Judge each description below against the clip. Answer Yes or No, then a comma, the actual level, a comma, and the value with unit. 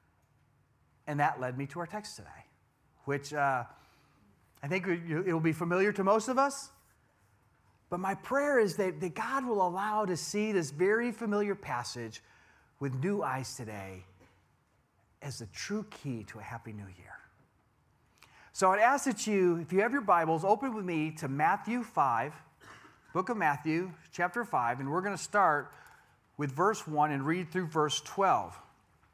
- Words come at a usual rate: Yes, average, 165 wpm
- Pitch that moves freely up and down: Yes, wide, 7.4 semitones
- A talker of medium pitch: Yes, medium, 165 Hz